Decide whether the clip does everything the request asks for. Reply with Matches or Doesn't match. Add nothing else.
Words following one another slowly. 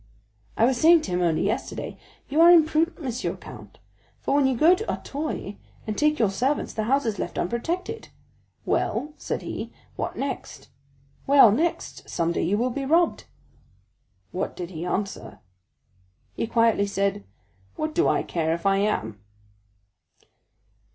Doesn't match